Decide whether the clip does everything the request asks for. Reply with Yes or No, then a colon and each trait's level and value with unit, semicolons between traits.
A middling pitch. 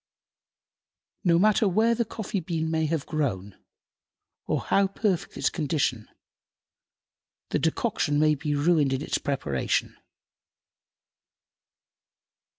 Yes: medium, 160 Hz